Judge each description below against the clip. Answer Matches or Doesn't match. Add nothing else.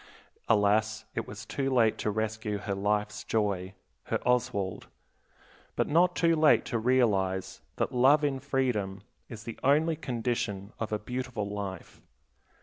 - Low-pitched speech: Matches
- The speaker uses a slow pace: Doesn't match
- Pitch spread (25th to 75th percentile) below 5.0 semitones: Matches